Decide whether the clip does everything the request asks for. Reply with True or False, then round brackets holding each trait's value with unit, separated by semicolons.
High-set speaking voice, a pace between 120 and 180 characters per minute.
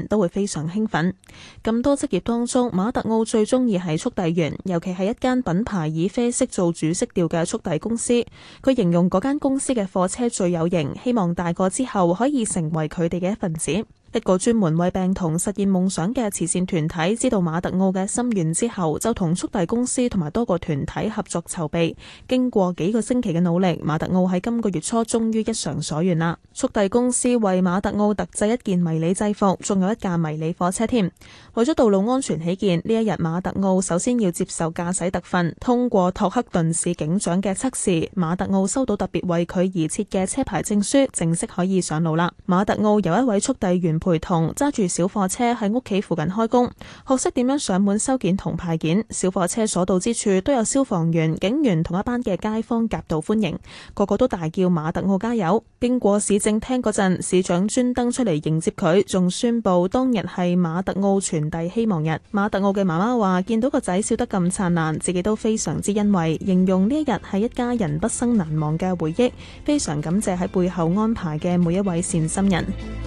False (195 Hz; 305 characters per minute)